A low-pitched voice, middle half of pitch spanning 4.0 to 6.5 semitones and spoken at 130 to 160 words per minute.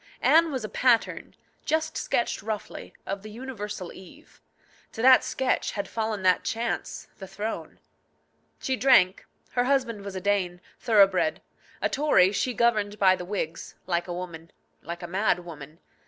No: high, 205 Hz; average, 4.7 semitones; average, 155 wpm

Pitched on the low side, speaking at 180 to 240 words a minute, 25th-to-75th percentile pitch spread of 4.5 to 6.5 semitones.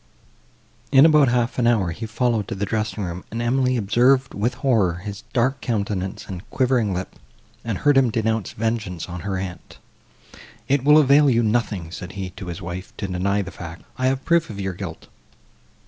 Yes: low, 110 Hz; average, 190 wpm; average, 5.0 semitones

